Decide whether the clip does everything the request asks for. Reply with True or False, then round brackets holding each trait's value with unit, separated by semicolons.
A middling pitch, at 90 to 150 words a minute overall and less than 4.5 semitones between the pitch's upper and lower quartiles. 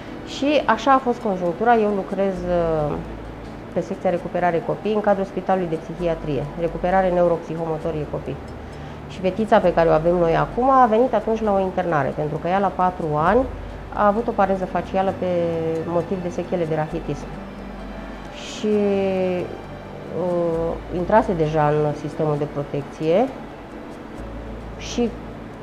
True (175 Hz; 140 wpm; 3.7 semitones)